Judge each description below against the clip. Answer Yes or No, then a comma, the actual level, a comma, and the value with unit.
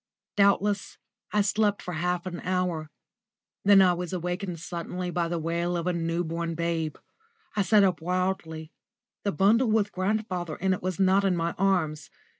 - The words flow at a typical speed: Yes, average, 170 wpm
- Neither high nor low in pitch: Yes, medium, 180 Hz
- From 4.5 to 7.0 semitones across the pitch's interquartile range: No, narrow, 2.5 semitones